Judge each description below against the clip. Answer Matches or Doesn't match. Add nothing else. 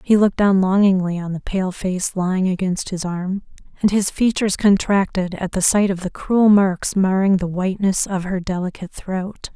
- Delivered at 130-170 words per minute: Doesn't match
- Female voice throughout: Matches